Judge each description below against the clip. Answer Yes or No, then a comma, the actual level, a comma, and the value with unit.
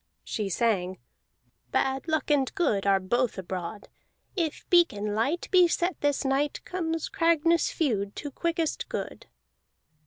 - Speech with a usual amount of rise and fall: No, wide, 8.2 semitones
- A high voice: Yes, very high, 275 Hz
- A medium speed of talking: No, slow, 130 wpm